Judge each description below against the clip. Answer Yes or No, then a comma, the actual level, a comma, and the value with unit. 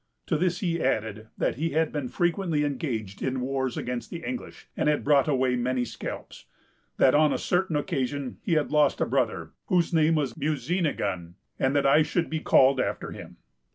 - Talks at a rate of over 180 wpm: Yes, average, 190 wpm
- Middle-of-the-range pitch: Yes, medium, 145 Hz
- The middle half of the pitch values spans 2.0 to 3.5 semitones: No, average, 4.0 semitones